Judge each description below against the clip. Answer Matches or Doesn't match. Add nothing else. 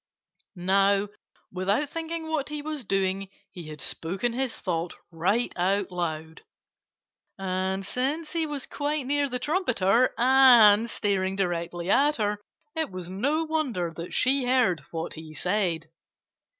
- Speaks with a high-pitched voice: Matches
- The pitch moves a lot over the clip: Matches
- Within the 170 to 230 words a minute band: Doesn't match